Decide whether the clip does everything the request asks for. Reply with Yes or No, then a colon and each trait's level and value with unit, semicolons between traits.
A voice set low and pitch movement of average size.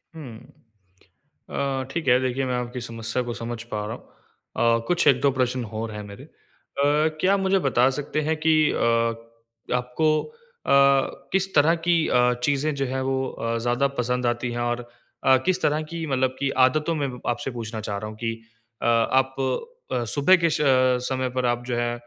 Yes: low, 125 Hz; average, 3.3 semitones